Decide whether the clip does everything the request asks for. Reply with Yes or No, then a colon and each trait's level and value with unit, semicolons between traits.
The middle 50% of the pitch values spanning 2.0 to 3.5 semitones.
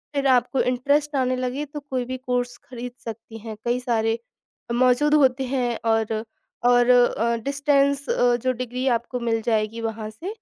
Yes: narrow, 2.5 semitones